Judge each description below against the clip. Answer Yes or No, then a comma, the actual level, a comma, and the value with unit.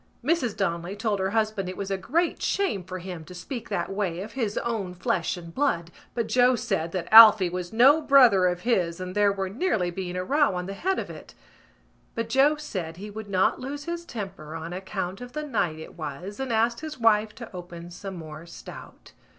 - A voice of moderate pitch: No, high, 200 Hz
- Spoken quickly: Yes, fast, 215 wpm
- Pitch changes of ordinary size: Yes, average, 5.0 semitones